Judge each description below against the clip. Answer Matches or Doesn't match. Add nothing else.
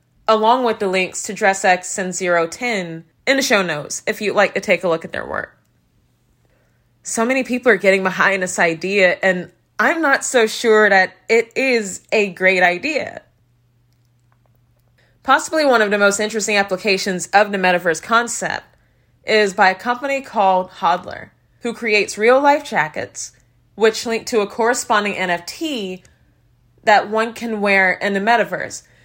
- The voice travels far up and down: Doesn't match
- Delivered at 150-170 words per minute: Matches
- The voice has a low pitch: Doesn't match